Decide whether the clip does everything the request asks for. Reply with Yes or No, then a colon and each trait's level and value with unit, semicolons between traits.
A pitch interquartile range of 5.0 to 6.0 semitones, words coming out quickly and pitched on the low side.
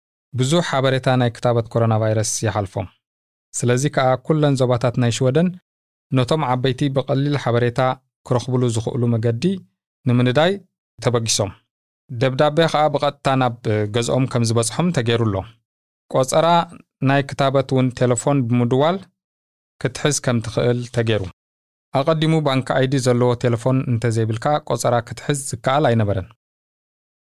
No: average, 3.2 semitones; fast, 115 wpm; low, 125 Hz